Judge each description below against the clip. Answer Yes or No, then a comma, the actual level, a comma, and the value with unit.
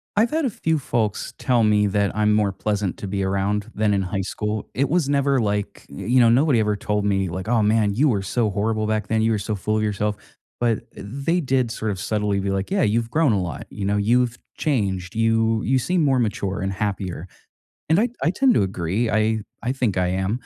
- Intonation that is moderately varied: Yes, average, 3.5 semitones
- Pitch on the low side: Yes, low, 110 Hz